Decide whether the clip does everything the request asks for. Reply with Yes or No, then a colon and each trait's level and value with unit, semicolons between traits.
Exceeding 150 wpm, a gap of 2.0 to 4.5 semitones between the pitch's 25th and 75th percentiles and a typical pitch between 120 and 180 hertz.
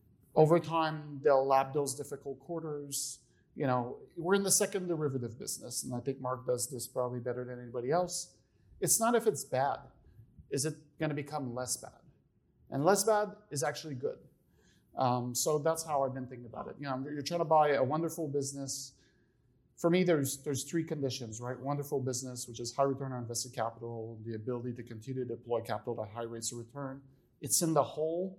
Yes: average, 200 wpm; average, 4.0 semitones; low, 135 Hz